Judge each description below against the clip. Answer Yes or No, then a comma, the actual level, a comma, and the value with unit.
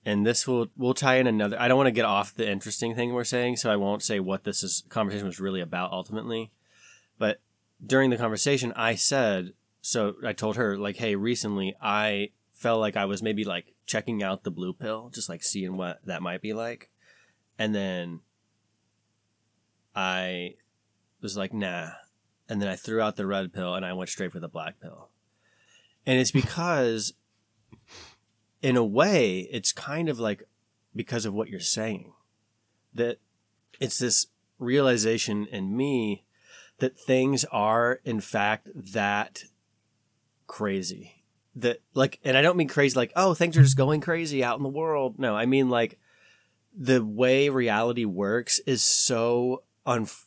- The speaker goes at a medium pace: Yes, average, 170 wpm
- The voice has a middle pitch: No, low, 110 Hz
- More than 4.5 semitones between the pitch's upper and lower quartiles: No, average, 3.3 semitones